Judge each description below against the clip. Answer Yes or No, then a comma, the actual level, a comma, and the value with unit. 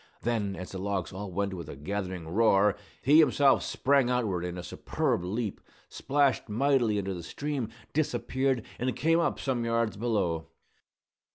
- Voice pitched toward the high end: No, low, 110 Hz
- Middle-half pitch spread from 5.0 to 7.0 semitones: Yes, wide, 5.6 semitones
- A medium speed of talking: Yes, average, 160 wpm